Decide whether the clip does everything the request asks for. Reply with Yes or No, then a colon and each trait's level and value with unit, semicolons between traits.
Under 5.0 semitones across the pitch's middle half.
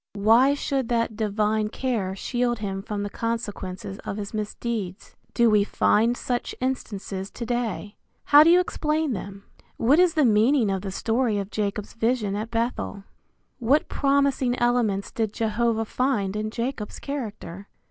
Yes: average, 3.4 semitones